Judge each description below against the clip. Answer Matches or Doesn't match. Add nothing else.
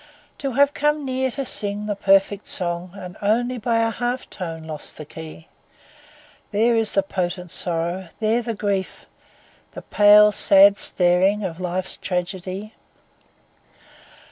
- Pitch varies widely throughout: Doesn't match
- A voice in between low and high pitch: Doesn't match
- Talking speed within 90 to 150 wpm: Matches